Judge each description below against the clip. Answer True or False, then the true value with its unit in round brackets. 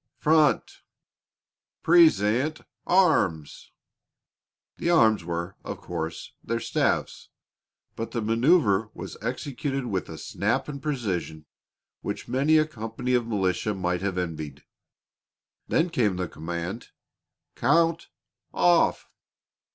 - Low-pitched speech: True (115 Hz)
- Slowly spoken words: True (105 wpm)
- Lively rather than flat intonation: True (8.8 semitones)